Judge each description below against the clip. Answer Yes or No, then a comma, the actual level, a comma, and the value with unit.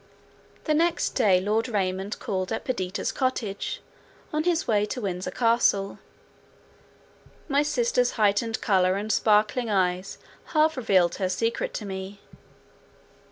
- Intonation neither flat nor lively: Yes, average, 4.4 semitones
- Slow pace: Yes, slow, 125 wpm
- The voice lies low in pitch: No, high, 210 Hz